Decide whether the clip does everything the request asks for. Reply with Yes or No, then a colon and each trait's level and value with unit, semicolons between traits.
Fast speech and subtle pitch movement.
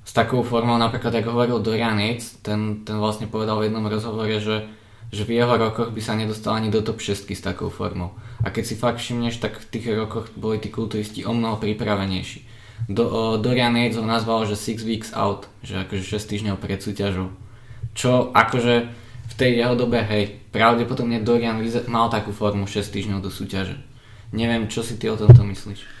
Yes: fast, 190 wpm; narrow, 1.9 semitones